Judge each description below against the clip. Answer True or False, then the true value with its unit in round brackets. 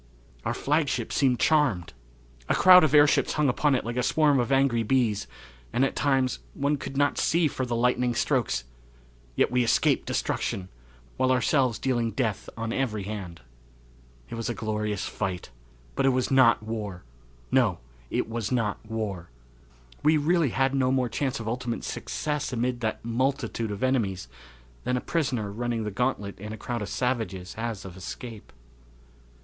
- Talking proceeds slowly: False (165 wpm)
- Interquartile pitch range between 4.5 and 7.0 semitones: False (3.7 semitones)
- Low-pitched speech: True (120 Hz)